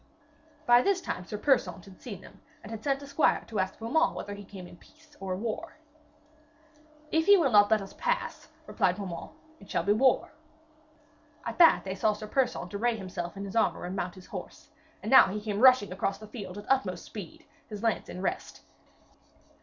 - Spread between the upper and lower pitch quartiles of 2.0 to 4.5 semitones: No, average, 5.1 semitones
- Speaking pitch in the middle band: No, high, 210 Hz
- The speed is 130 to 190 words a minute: No, average, 200 wpm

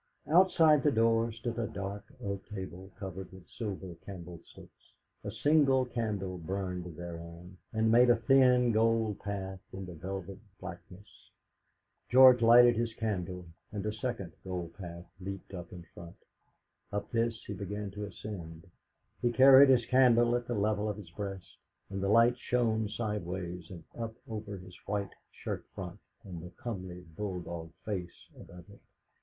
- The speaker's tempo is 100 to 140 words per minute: No, average, 155 wpm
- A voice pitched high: No, low, 100 Hz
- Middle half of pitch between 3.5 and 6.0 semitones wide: Yes, average, 4.0 semitones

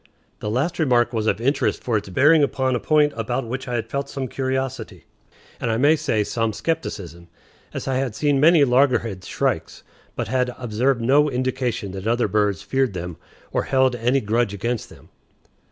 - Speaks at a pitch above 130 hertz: No, low, 125 Hz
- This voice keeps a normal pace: Yes, average, 185 wpm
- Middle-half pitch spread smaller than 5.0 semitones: Yes, average, 3.5 semitones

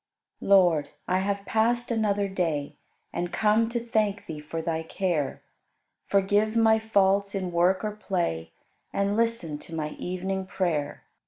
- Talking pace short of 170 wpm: Yes, average, 145 wpm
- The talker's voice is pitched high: Yes, high, 195 Hz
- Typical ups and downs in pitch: Yes, average, 3.8 semitones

